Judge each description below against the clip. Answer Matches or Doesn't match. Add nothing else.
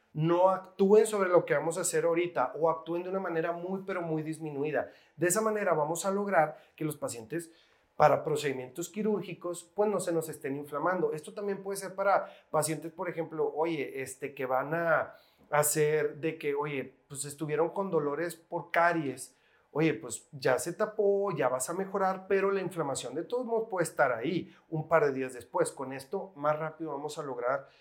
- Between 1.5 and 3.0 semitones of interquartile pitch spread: Doesn't match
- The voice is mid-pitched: Matches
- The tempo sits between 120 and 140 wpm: Doesn't match